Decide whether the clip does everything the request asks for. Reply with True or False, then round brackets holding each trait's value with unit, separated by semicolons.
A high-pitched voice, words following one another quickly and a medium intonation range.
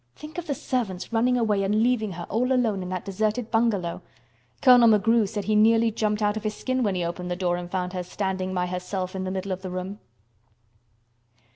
True (205 Hz; 220 wpm; 3.6 semitones)